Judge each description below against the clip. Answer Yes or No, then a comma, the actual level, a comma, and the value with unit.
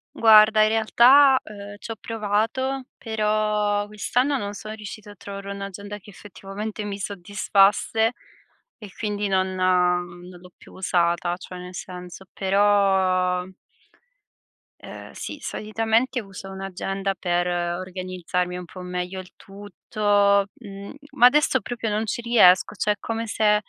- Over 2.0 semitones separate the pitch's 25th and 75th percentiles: Yes, narrow, 2.6 semitones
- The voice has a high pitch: Yes, high, 205 Hz